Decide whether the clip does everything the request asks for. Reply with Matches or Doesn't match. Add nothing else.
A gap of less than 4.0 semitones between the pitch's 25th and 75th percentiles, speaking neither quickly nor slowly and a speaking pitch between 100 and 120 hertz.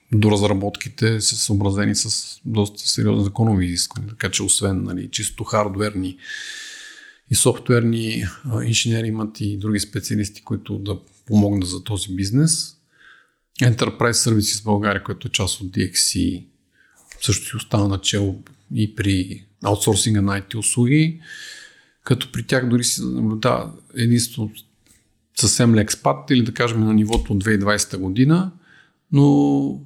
Matches